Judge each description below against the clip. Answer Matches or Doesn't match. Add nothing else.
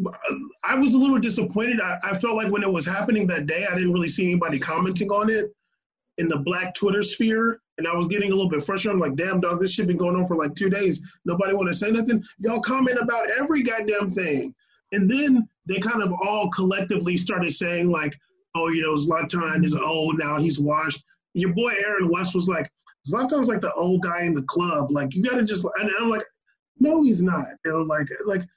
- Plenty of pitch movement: Doesn't match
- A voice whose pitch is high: Matches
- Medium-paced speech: Doesn't match